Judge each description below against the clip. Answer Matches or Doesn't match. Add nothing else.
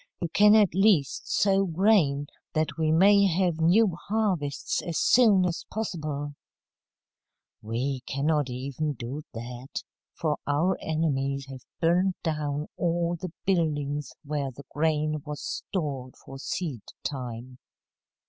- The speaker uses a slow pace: Matches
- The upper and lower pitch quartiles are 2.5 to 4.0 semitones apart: Doesn't match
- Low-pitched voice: Doesn't match